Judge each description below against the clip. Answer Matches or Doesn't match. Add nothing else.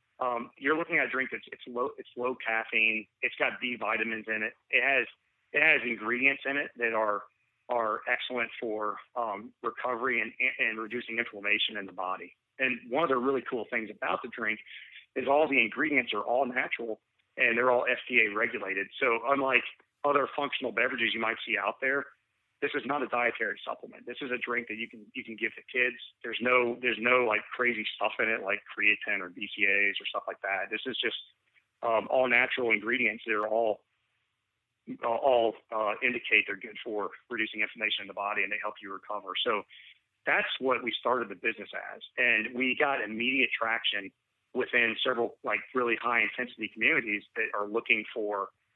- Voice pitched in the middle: Doesn't match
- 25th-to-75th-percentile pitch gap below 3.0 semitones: Matches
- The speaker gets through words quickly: Doesn't match